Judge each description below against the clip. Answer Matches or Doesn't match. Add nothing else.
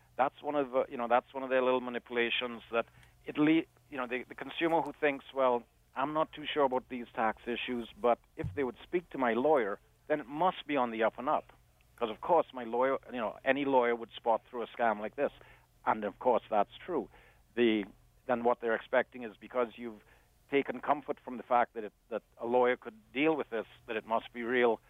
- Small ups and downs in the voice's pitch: Doesn't match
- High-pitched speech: Doesn't match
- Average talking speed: Doesn't match